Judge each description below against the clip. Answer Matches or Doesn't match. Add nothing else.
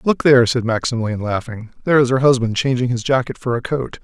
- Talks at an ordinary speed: Doesn't match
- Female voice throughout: Doesn't match